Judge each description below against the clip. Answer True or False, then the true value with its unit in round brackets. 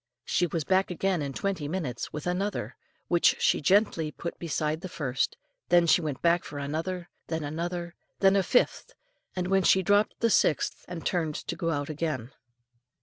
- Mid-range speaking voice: True (170 Hz)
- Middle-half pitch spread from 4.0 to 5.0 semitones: False (3.5 semitones)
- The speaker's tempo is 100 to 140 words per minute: False (180 wpm)